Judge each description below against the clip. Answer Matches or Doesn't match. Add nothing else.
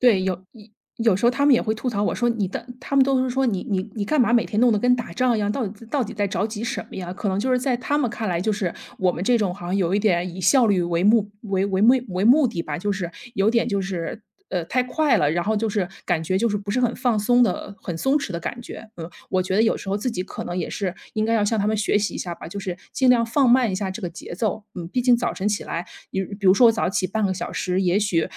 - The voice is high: Matches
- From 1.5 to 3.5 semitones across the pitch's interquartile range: Doesn't match